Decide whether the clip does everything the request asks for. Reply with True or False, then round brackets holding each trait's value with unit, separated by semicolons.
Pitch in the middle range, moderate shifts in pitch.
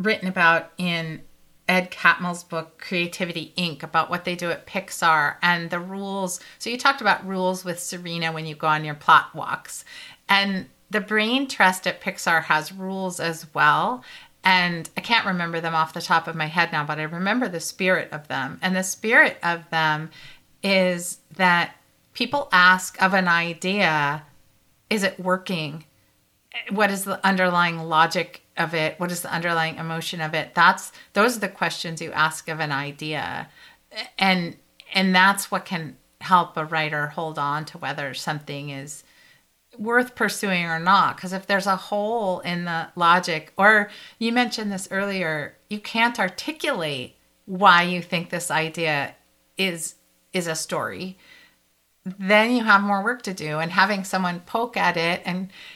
True (180 Hz; 3.1 semitones)